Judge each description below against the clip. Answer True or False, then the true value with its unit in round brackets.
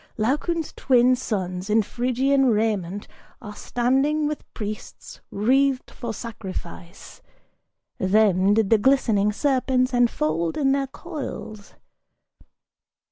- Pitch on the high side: True (235 Hz)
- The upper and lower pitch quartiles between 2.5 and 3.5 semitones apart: False (4.6 semitones)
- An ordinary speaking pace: False (100 wpm)